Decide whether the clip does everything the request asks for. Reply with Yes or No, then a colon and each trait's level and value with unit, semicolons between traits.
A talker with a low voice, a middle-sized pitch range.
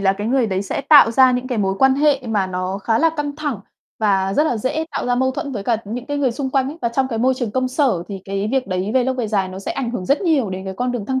No: high, 245 Hz; average, 5.0 semitones